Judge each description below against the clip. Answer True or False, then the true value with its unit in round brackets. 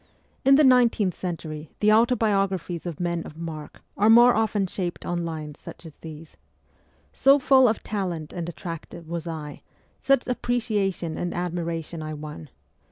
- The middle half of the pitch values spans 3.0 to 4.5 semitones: False (5.1 semitones)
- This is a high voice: False (175 Hz)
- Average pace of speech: True (160 wpm)